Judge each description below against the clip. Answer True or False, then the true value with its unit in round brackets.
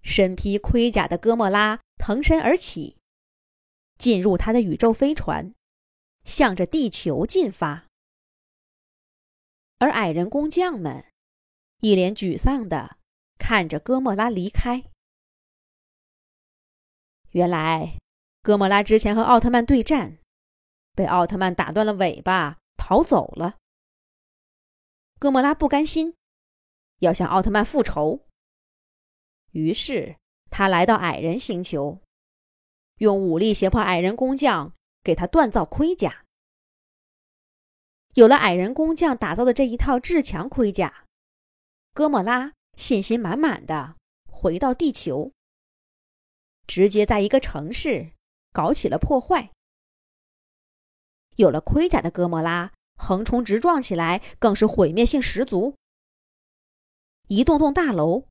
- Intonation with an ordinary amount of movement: False (6.5 semitones)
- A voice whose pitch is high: True (220 Hz)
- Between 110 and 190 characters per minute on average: True (175 characters per minute)